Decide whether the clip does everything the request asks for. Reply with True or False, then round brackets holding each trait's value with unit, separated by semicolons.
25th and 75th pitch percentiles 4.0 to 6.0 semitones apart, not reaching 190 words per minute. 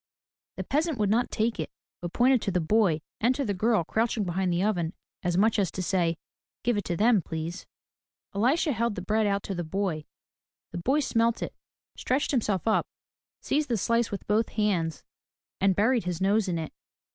False (4.6 semitones; 195 wpm)